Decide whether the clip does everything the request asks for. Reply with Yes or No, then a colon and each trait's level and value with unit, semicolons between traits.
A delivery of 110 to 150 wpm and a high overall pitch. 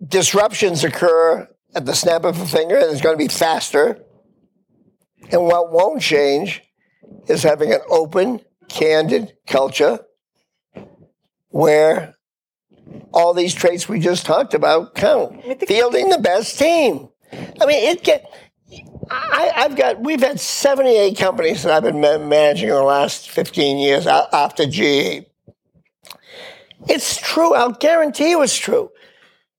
Yes: slow, 135 wpm; high, 205 Hz